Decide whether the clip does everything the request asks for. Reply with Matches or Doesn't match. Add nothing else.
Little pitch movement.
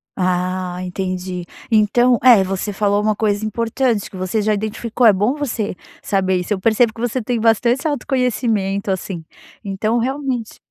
Doesn't match